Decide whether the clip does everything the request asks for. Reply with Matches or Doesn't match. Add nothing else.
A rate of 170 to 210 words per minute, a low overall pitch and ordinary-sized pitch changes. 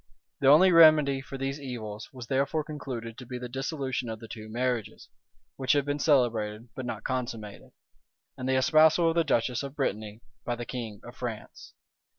Matches